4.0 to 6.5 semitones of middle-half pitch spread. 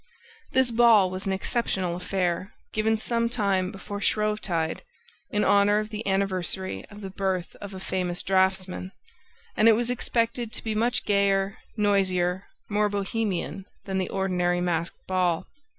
No: narrow, 2.4 semitones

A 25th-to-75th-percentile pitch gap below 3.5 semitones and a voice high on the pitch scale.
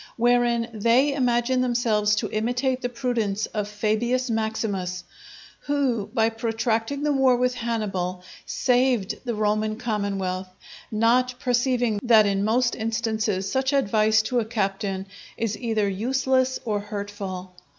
Yes: average, 3.0 semitones; high, 225 Hz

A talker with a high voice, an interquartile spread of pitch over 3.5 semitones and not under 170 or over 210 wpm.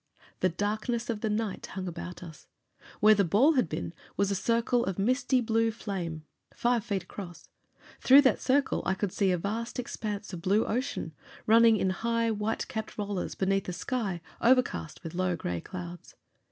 Yes: high, 205 Hz; average, 4.1 semitones; average, 180 wpm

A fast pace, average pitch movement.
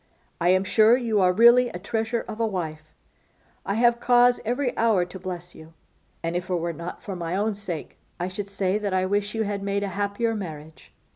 Yes: fast, 215 wpm; average, 3.8 semitones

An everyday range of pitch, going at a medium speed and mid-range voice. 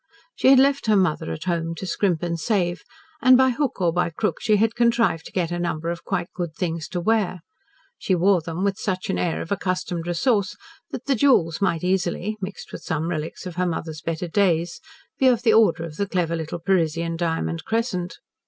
No: average, 3.9 semitones; fast, 210 wpm; medium, 180 Hz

